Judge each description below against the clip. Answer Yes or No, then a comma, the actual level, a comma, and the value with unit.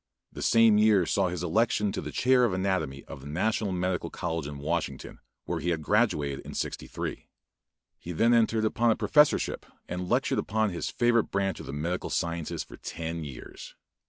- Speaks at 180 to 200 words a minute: Yes, average, 185 wpm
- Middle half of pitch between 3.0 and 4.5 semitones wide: No, average, 4.9 semitones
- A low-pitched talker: Yes, very low, 90 Hz